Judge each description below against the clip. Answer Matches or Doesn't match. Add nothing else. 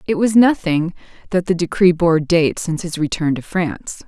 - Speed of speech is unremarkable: Matches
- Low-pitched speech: Doesn't match